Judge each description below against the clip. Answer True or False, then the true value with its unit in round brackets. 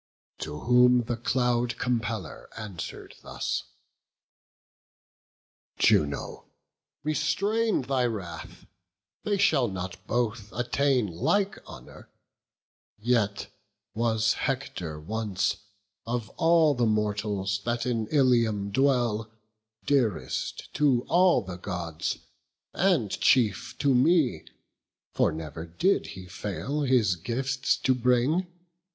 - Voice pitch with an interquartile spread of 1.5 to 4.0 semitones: False (4.7 semitones)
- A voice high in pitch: False (120 Hz)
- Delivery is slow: True (100 wpm)